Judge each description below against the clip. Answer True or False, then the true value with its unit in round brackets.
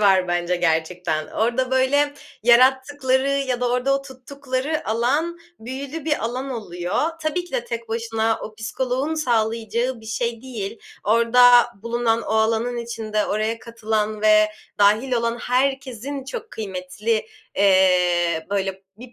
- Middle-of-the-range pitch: False (235 Hz)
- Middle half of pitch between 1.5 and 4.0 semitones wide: True (3.6 semitones)